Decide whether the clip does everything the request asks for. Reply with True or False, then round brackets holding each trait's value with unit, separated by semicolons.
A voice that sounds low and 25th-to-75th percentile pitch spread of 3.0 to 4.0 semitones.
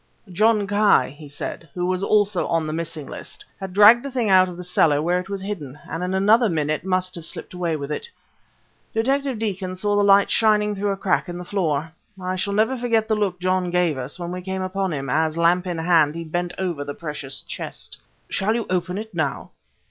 False (185 Hz; 3.6 semitones)